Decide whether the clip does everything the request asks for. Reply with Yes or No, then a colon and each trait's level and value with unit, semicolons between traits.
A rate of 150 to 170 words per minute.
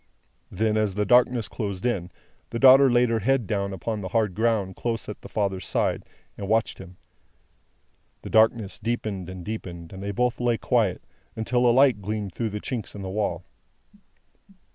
No: average, 180 wpm